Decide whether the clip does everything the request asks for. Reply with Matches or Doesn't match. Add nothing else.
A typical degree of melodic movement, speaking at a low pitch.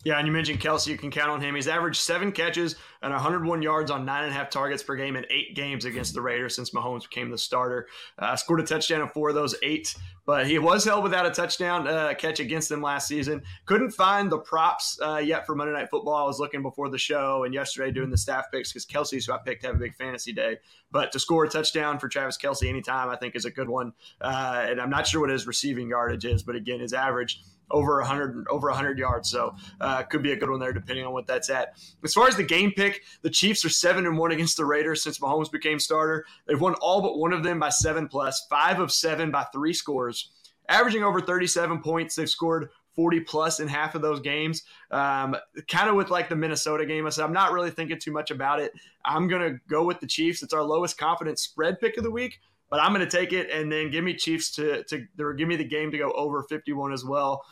Doesn't match